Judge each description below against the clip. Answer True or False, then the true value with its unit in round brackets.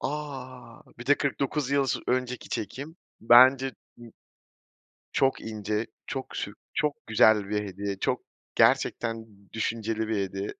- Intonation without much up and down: False (3.8 semitones)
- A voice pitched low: True (115 Hz)